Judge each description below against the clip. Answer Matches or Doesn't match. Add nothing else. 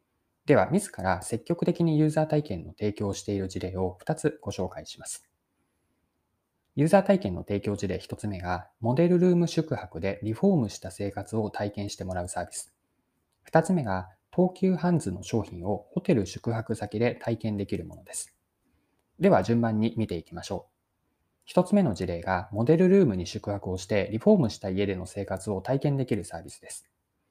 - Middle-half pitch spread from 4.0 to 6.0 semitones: Doesn't match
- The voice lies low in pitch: Matches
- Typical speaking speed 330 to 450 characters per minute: Matches